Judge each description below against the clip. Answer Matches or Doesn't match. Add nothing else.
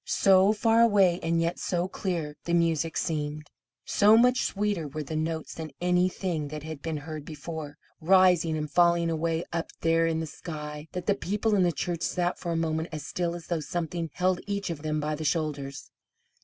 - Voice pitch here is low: Doesn't match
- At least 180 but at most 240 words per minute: Matches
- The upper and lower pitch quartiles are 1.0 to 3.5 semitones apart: Matches